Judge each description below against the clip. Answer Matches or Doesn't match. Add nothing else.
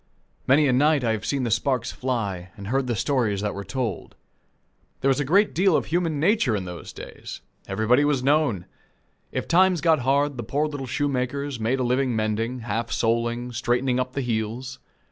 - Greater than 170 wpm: Matches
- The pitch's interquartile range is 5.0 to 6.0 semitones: Doesn't match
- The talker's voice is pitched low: Matches